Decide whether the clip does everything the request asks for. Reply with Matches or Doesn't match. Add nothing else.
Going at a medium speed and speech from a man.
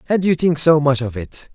Doesn't match